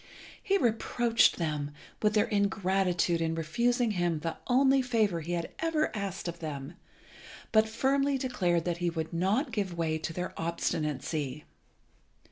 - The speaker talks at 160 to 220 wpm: No, average, 145 wpm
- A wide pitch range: Yes, wide, 5.8 semitones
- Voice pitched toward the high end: No, medium, 180 Hz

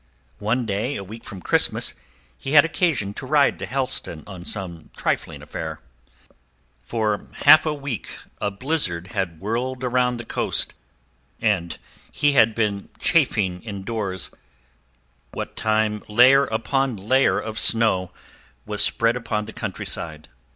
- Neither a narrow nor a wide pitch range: Yes, average, 4.5 semitones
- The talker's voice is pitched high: No, low, 110 Hz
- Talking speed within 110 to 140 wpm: Yes, slow, 135 wpm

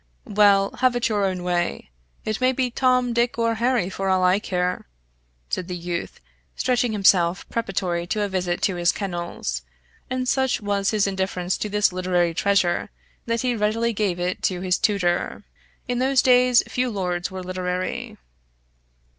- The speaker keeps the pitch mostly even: No, average, 4.5 semitones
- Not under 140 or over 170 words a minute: Yes, average, 165 wpm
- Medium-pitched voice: No, high, 195 Hz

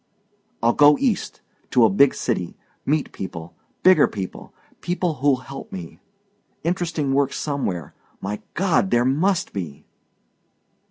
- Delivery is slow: Yes, slow, 125 wpm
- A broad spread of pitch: Yes, wide, 8.9 semitones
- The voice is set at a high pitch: No, low, 135 Hz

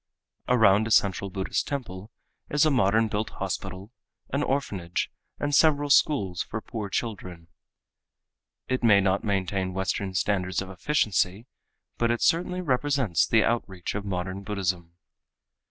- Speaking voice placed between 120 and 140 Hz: No, low, 100 Hz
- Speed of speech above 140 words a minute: No, slow, 135 wpm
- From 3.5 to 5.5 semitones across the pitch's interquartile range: Yes, average, 5.0 semitones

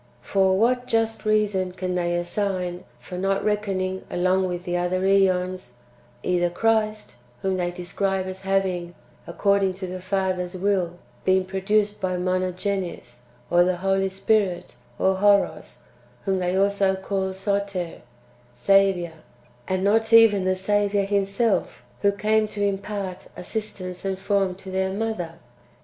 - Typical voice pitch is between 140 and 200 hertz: Yes, high, 190 Hz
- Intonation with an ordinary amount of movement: No, narrow, 1.7 semitones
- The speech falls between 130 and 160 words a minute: Yes, slow, 135 wpm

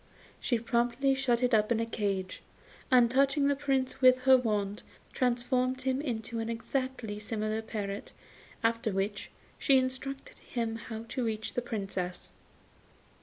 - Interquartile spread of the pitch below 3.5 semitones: Yes, average, 3.0 semitones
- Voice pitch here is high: Yes, high, 235 Hz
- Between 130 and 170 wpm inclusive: Yes, average, 145 wpm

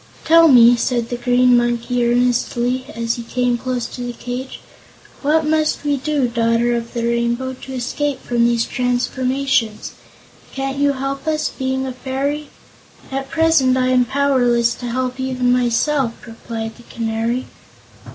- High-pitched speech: Yes, very high, 250 Hz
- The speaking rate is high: No, average, 150 wpm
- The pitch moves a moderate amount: No, narrow, 2.2 semitones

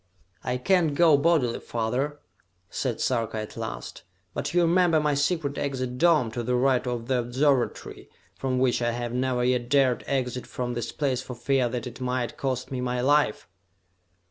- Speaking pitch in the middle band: No, low, 125 Hz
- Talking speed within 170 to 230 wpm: Yes, average, 175 wpm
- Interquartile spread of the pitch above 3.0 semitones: No, average, 2.7 semitones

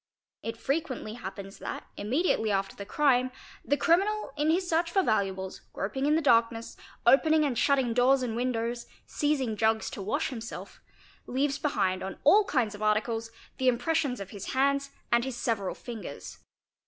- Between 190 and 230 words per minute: No, average, 165 wpm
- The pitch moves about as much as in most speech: Yes, average, 4.9 semitones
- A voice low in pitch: No, high, 245 Hz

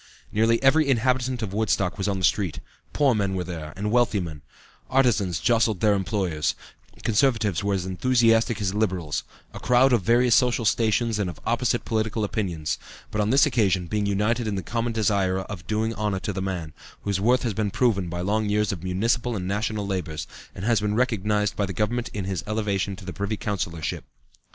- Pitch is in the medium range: No, low, 105 Hz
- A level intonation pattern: No, average, 3.3 semitones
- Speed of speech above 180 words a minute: Yes, average, 195 wpm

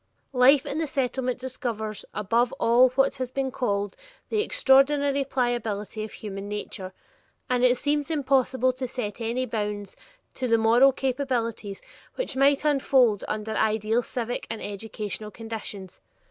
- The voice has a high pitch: Yes, high, 245 Hz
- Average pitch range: Yes, average, 3.7 semitones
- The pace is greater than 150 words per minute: No, average, 140 wpm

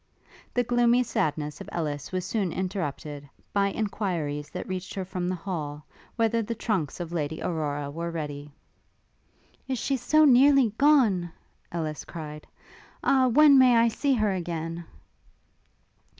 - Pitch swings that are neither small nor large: No, wide, 7.0 semitones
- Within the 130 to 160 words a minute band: Yes, average, 140 wpm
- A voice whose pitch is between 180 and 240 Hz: Yes, medium, 185 Hz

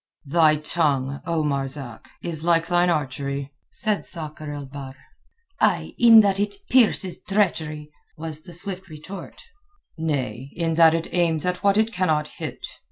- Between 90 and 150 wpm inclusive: Yes, average, 140 wpm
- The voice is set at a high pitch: No, medium, 160 Hz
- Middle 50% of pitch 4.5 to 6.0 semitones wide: No, average, 3.8 semitones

